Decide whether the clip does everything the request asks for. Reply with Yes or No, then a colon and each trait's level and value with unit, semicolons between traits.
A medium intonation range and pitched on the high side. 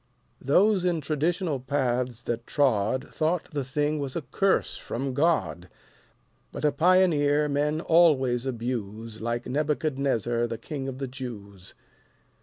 No: average, 4.2 semitones; low, 135 Hz